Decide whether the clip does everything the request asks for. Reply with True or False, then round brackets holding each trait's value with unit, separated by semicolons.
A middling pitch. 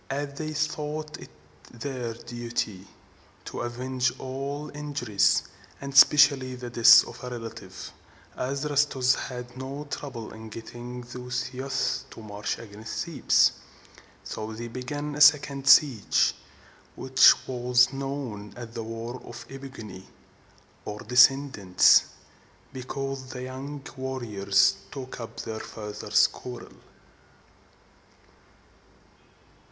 False (125 Hz)